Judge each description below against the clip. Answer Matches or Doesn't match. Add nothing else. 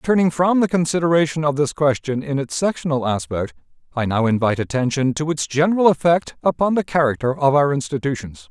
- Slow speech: Doesn't match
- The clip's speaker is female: Doesn't match